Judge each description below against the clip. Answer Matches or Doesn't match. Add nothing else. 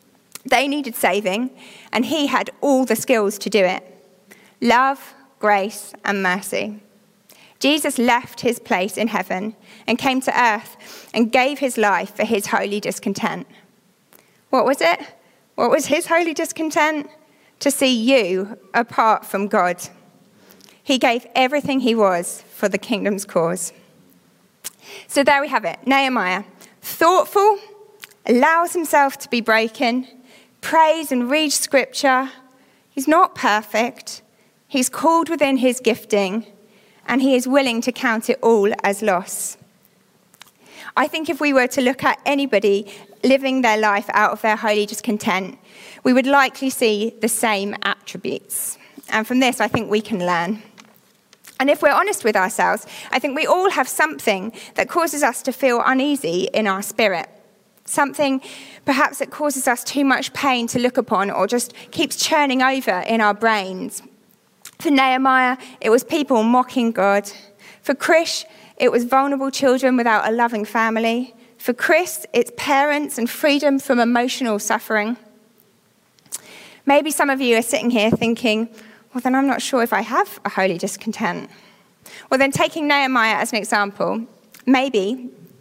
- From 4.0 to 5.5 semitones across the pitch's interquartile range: Matches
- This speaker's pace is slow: Doesn't match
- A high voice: Matches